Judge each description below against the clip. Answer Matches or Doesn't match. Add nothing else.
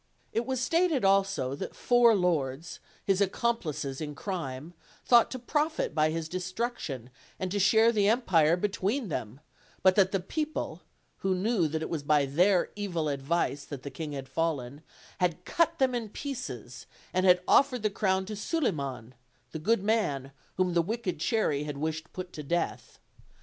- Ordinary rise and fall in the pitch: Doesn't match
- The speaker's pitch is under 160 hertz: Doesn't match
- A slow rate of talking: Doesn't match